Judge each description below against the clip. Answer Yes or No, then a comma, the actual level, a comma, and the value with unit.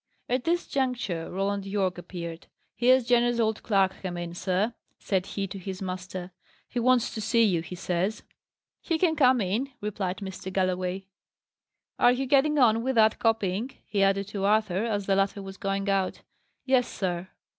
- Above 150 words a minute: Yes, average, 175 wpm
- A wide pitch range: No, average, 4.2 semitones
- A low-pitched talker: No, high, 200 Hz